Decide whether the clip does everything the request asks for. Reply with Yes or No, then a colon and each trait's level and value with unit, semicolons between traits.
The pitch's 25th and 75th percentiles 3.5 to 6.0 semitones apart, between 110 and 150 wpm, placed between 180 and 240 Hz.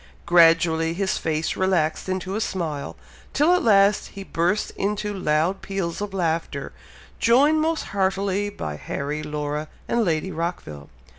Yes: average, 3.9 semitones; average, 140 wpm; medium, 185 Hz